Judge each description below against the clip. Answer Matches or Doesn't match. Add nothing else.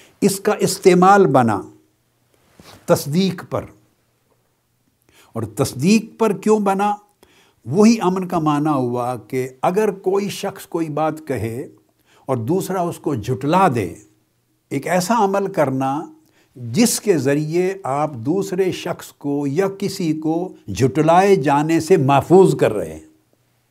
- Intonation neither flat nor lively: Doesn't match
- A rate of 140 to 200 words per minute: Doesn't match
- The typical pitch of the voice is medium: Matches